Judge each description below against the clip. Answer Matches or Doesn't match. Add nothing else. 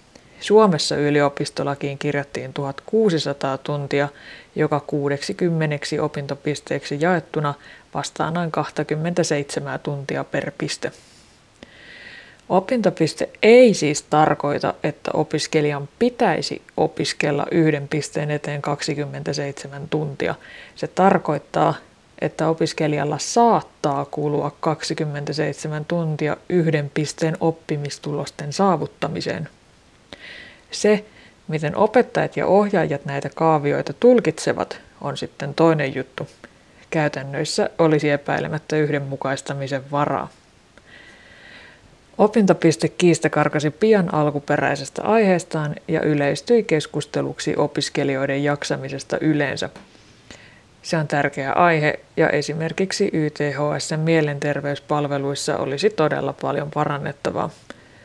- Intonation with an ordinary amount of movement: Doesn't match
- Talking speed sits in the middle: Doesn't match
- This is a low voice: Doesn't match